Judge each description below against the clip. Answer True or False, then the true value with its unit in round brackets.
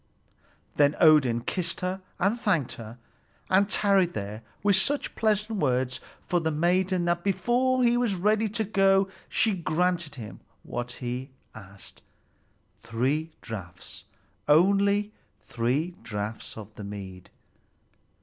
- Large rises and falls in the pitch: True (8.5 semitones)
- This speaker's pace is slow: True (125 wpm)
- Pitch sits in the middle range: True (170 Hz)